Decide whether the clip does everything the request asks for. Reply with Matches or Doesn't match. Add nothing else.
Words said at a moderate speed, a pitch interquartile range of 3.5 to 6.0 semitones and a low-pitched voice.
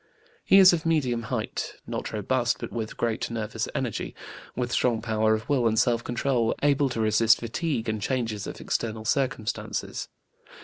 Doesn't match